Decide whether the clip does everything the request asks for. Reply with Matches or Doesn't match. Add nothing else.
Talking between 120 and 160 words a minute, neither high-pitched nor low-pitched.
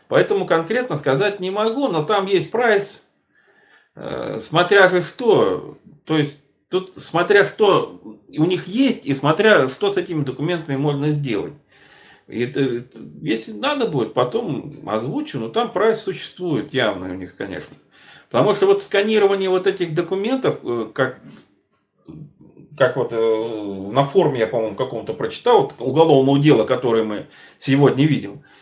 Matches